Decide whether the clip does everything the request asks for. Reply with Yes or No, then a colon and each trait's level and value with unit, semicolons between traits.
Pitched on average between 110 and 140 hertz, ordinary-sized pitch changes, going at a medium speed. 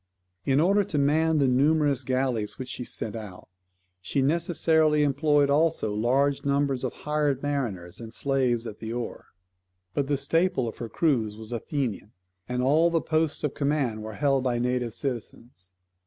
Yes: low, 135 Hz; average, 3.9 semitones; average, 160 wpm